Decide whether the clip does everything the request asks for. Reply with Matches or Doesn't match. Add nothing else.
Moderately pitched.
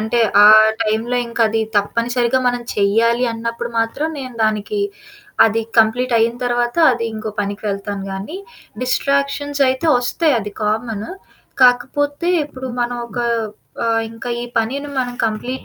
Doesn't match